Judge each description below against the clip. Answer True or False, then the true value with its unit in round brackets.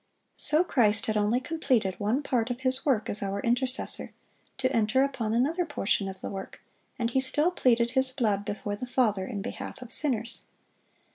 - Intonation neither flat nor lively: True (3.9 semitones)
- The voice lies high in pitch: True (240 Hz)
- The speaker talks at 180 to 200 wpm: True (185 wpm)